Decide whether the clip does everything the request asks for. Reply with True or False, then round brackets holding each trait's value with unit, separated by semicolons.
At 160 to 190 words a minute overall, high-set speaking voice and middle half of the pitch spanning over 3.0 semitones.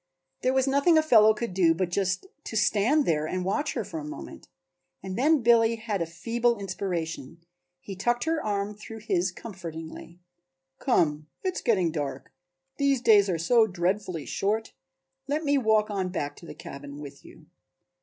True (175 wpm; 205 Hz; 5.6 semitones)